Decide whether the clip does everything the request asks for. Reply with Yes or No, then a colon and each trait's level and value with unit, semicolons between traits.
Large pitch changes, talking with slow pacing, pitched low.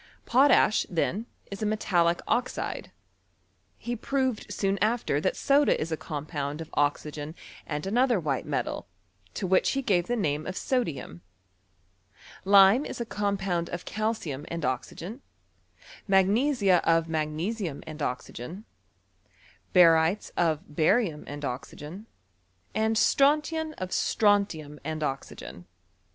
No: wide, 6.0 semitones; slow, 125 wpm; medium, 185 Hz